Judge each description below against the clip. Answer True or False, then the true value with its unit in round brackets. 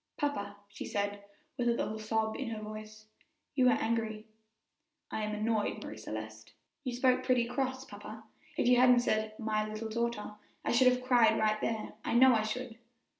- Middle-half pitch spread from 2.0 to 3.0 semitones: True (2.5 semitones)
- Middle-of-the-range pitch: False (220 Hz)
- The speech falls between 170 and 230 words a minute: True (180 wpm)